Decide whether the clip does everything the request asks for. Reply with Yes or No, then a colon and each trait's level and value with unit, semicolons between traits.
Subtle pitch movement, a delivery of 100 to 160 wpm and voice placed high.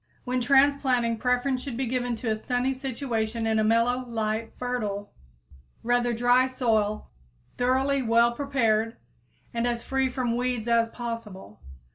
Yes: narrow, 2.0 semitones; average, 140 wpm; high, 240 Hz